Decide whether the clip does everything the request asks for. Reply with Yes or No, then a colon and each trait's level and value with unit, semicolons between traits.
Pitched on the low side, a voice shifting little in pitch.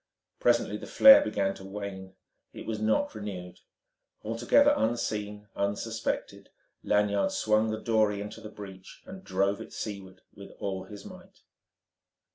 Yes: low, 105 Hz; narrow, 2.0 semitones